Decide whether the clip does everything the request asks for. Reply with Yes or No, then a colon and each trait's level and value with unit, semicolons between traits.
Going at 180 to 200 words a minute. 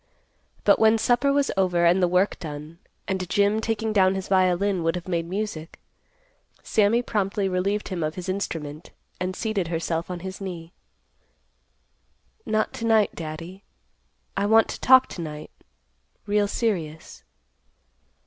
No: average, 145 wpm